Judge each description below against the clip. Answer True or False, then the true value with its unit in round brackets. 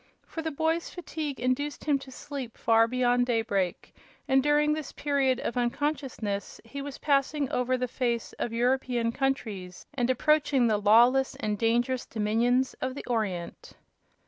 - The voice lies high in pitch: True (255 Hz)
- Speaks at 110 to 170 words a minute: True (150 wpm)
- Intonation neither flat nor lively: True (3.4 semitones)